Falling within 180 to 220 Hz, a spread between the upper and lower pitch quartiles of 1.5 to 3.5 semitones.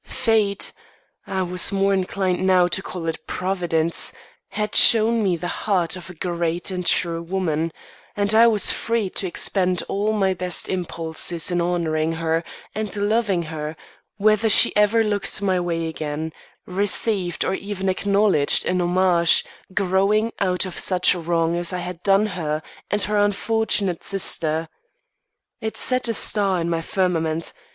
Yes: medium, 185 Hz; average, 3.1 semitones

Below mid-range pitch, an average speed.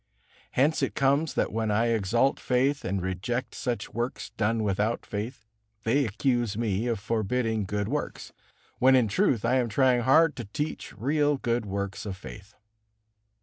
Yes: low, 115 Hz; average, 160 wpm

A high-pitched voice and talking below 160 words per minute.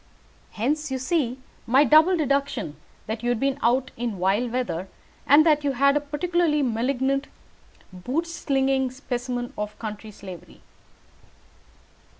Yes: very high, 260 Hz; average, 140 wpm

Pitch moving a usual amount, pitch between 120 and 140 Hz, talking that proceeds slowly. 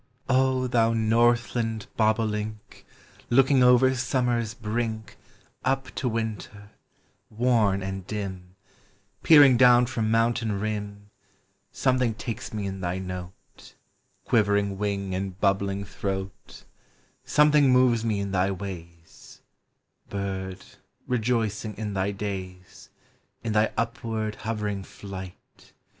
No: average, 3.3 semitones; low, 110 Hz; slow, 110 wpm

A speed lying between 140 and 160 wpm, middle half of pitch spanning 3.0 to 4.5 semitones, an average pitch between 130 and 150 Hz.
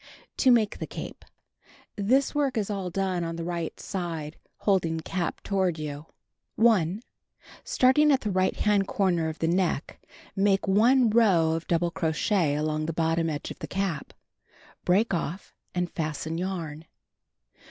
No: average, 150 wpm; average, 3.9 semitones; medium, 180 Hz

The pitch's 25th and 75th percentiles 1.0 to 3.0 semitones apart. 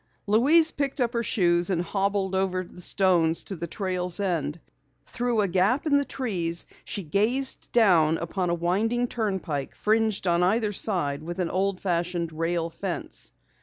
No: average, 4.2 semitones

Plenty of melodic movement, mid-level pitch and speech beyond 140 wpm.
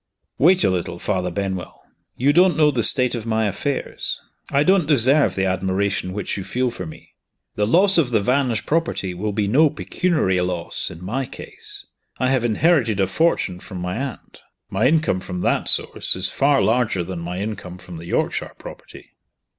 No: wide, 7.0 semitones; low, 110 Hz; average, 185 wpm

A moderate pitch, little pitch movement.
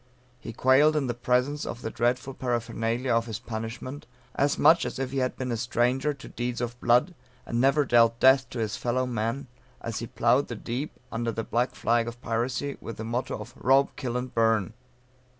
No: low, 120 Hz; narrow, 2.3 semitones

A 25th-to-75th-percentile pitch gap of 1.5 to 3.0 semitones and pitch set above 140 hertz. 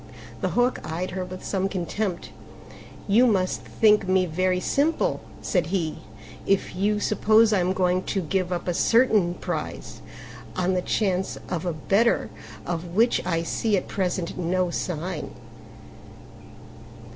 Yes: average, 2.7 semitones; medium, 185 Hz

